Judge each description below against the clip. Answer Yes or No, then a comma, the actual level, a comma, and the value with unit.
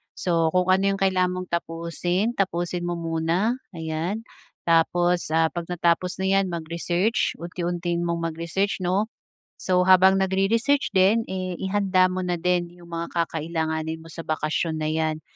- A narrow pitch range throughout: Yes, narrow, 2.2 semitones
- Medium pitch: Yes, medium, 175 Hz